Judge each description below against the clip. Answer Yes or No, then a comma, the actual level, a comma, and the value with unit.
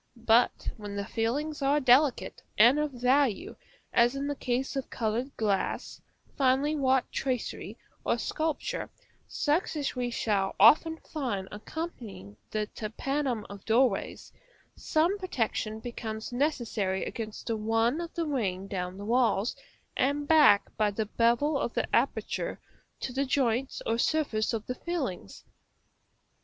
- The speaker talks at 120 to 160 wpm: Yes, average, 140 wpm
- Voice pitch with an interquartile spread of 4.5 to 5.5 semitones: Yes, average, 4.8 semitones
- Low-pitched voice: No, high, 245 Hz